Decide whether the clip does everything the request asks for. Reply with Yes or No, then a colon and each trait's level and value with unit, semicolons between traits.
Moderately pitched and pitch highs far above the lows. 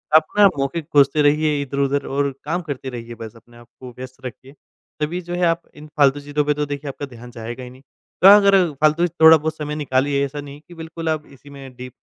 No: medium, 145 Hz; average, 2.9 semitones